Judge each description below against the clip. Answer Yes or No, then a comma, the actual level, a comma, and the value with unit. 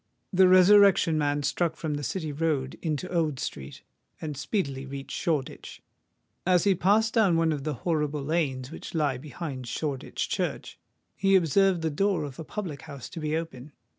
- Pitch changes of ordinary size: Yes, average, 4.1 semitones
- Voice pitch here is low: No, medium, 155 Hz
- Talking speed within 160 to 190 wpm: Yes, average, 170 wpm